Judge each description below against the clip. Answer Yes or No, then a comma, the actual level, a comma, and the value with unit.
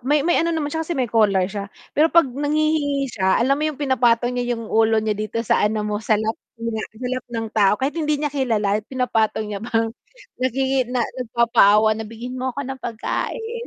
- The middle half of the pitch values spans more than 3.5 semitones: Yes, average, 4.2 semitones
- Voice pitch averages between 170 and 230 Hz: No, high, 240 Hz